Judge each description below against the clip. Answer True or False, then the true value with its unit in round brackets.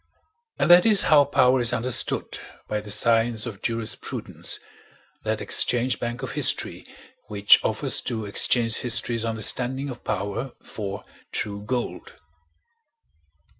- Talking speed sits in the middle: False (125 wpm)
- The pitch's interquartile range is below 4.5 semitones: True (3.0 semitones)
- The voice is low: True (120 Hz)